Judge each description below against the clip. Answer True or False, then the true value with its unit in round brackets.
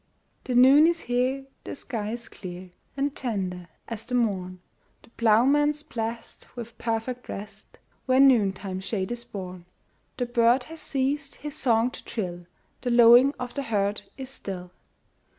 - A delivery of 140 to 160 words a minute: True (150 wpm)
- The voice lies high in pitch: True (235 Hz)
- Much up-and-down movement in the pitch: False (4.5 semitones)